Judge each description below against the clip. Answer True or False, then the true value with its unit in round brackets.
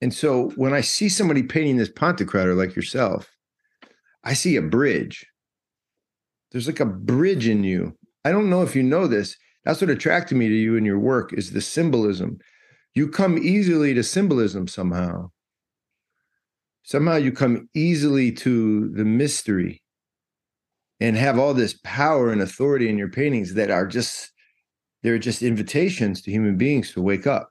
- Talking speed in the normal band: True (165 wpm)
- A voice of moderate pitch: False (125 Hz)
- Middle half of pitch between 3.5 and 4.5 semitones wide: False (5.5 semitones)